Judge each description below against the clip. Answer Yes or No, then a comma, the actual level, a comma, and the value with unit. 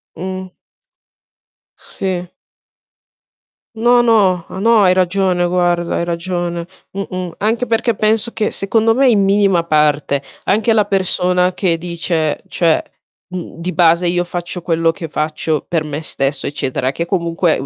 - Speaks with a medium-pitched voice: Yes, medium, 180 Hz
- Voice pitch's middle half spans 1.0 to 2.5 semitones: No, average, 2.9 semitones